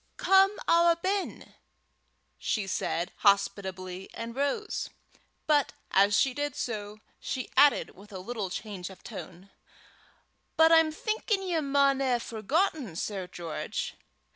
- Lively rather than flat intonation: Yes, wide, 8.3 semitones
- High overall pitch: Yes, high, 235 Hz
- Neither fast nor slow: No, slow, 125 wpm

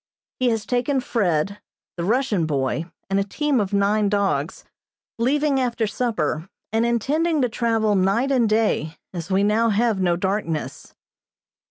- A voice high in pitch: Yes, high, 215 Hz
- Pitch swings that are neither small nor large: Yes, average, 4.2 semitones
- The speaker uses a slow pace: No, average, 150 wpm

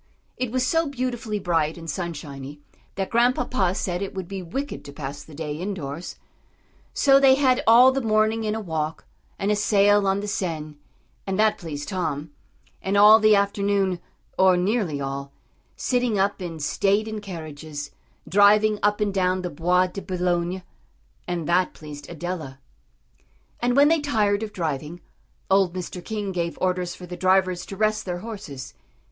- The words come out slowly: No, average, 165 wpm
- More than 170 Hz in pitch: Yes, high, 190 Hz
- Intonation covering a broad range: No, average, 4.2 semitones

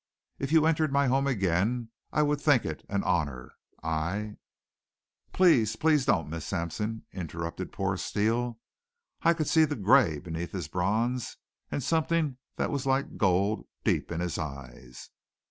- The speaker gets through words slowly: No, average, 155 wpm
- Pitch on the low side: Yes, low, 110 Hz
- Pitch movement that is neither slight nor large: No, wide, 8.4 semitones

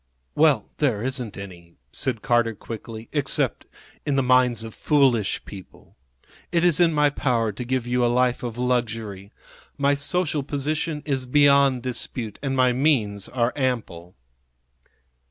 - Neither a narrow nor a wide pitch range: Yes, average, 3.8 semitones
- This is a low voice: Yes, low, 125 Hz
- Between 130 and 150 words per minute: Yes, average, 145 wpm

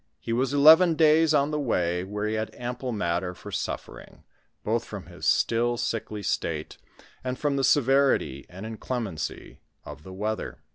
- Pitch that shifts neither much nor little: No, wide, 6.6 semitones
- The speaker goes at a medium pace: Yes, average, 170 wpm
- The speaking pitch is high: No, low, 115 Hz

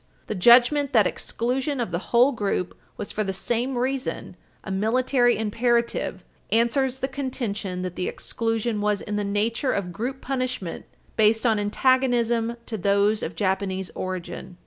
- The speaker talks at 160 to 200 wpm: No, average, 150 wpm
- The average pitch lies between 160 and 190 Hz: No, high, 225 Hz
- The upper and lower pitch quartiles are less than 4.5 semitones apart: Yes, average, 3.8 semitones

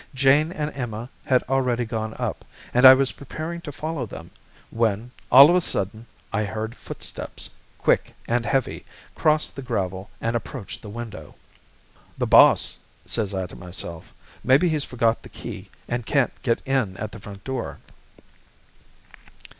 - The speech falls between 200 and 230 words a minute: No, average, 155 wpm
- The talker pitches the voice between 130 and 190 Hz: No, low, 120 Hz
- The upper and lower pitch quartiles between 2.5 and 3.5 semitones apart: No, average, 3.9 semitones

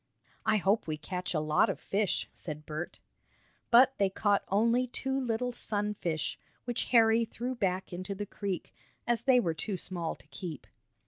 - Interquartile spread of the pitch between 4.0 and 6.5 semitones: Yes, average, 4.7 semitones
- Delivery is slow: No, average, 175 wpm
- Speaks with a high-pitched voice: Yes, high, 205 Hz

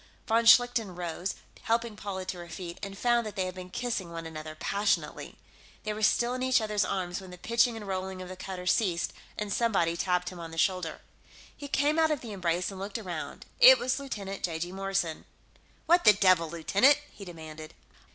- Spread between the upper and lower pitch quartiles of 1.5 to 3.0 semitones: No, average, 4.4 semitones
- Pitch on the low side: No, high, 195 Hz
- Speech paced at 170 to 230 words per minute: Yes, average, 200 wpm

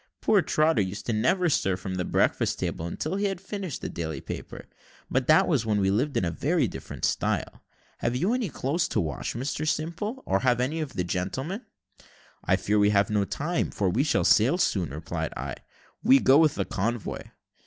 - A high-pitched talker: No, low, 125 Hz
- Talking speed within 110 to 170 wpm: No, average, 195 wpm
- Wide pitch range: Yes, wide, 8.7 semitones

